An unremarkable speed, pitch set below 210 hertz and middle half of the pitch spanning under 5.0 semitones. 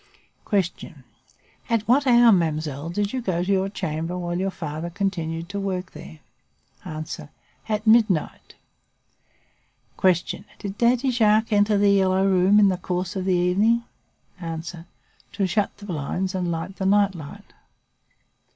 Yes: average, 145 wpm; high, 190 Hz; average, 3.1 semitones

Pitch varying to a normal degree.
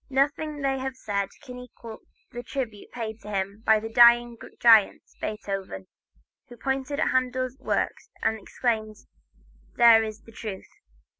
Yes: average, 3.2 semitones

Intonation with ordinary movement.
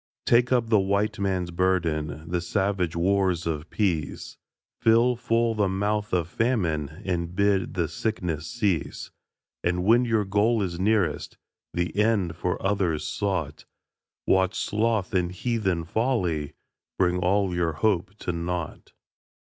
Yes: average, 3.7 semitones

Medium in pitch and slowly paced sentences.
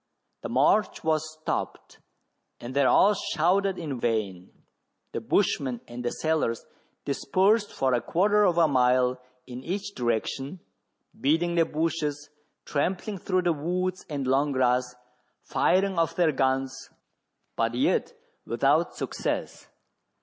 Yes: medium, 150 Hz; slow, 130 wpm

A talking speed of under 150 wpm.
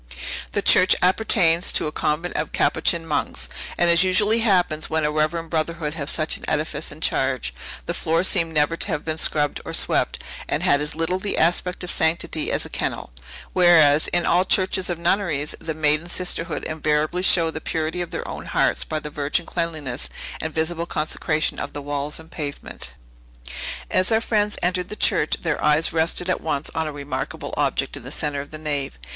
No: average, 195 wpm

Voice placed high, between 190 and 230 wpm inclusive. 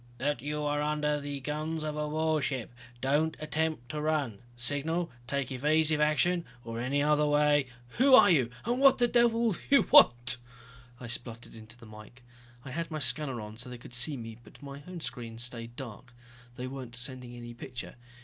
No: medium, 140 Hz; average, 195 wpm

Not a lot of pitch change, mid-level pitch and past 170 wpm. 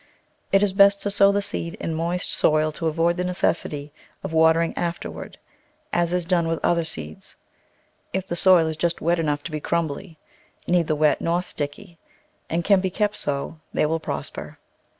Yes: narrow, 2.3 semitones; medium, 170 Hz; average, 180 wpm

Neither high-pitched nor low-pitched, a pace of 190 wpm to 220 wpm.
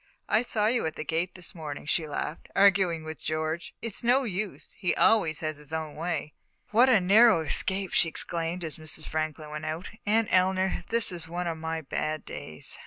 Yes: medium, 170 Hz; average, 195 wpm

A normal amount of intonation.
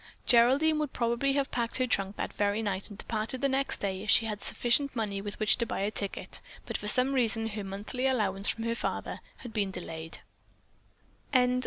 Yes: average, 3.9 semitones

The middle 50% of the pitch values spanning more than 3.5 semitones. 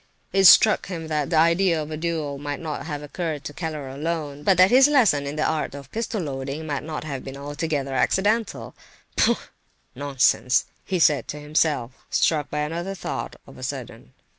No: average, 2.9 semitones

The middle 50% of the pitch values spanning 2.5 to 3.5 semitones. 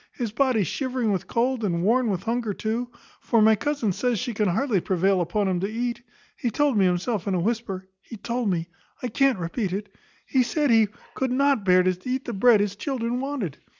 No: average, 4.4 semitones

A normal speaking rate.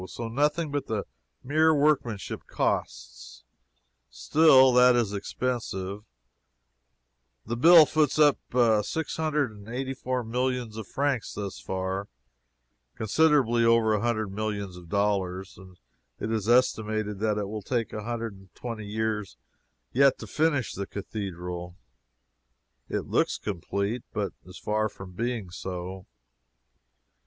No: slow, 130 wpm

